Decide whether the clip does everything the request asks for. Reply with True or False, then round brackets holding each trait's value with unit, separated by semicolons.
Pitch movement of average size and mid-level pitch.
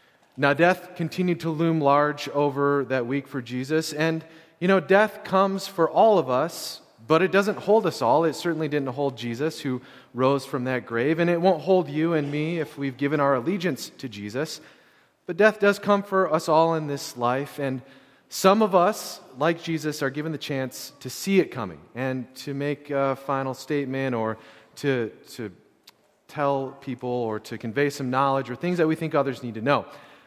True (4.0 semitones; 145 Hz)